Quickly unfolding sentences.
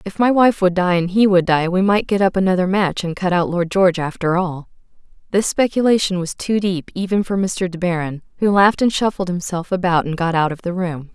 Yes: fast, 235 wpm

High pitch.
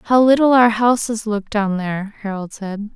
Yes: high, 215 Hz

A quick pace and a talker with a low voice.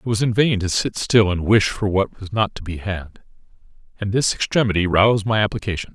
Yes: fast, 220 wpm; low, 100 Hz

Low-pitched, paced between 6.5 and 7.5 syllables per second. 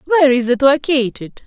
No: very high, 270 Hz; 6.9 syllables/s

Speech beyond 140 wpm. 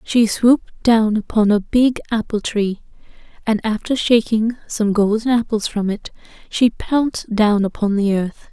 Yes: average, 155 wpm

